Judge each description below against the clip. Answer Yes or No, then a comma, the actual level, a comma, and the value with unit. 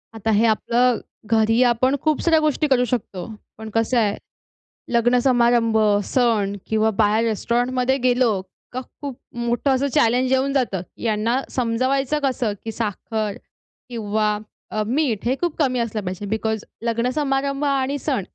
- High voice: Yes, high, 240 Hz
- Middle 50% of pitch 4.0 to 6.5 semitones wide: No, average, 3.0 semitones